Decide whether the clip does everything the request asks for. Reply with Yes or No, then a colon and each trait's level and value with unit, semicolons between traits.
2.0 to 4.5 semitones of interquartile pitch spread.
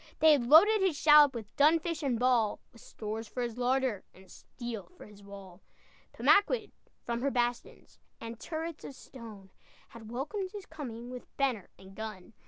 No: wide, 5.4 semitones